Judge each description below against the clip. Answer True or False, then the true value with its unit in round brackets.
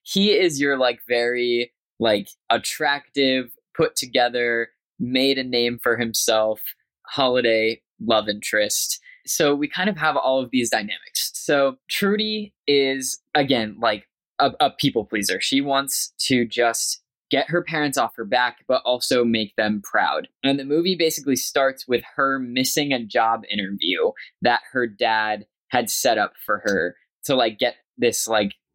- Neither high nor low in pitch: False (130 Hz)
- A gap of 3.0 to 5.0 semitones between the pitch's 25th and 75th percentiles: True (3.6 semitones)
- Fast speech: False (155 wpm)